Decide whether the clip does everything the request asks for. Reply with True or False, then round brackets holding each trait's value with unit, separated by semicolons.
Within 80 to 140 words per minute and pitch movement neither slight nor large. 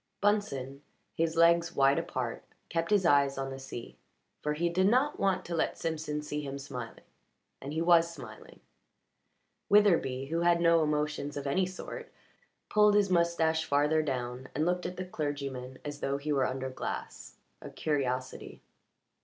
False (160 wpm; 3.8 semitones)